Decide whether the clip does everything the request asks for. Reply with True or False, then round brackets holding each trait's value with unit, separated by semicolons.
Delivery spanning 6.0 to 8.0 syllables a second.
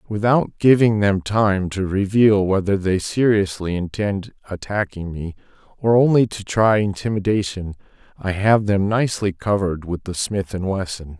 False (4.7 syllables/s)